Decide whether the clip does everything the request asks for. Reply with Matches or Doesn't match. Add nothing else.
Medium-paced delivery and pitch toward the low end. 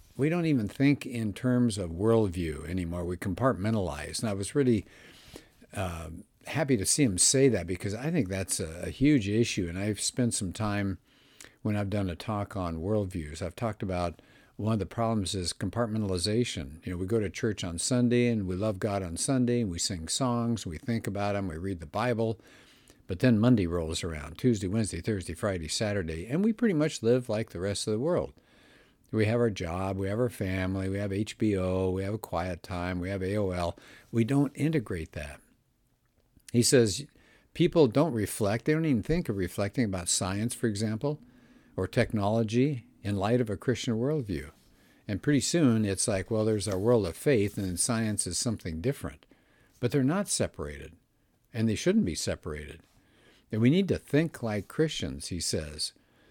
Matches